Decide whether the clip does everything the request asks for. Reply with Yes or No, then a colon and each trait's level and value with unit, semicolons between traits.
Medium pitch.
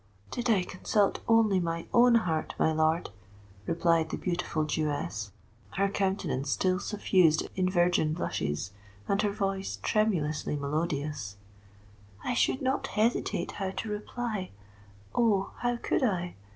Yes: medium, 180 Hz